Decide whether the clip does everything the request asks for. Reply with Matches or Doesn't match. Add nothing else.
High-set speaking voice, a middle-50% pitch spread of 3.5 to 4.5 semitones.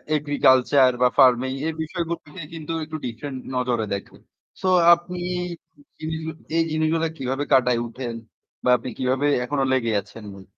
Doesn't match